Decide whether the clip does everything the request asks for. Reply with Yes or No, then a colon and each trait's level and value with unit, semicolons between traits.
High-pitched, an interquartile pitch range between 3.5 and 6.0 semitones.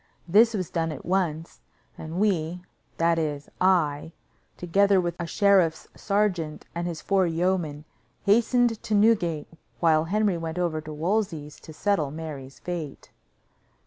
No: medium, 170 Hz; average, 3.9 semitones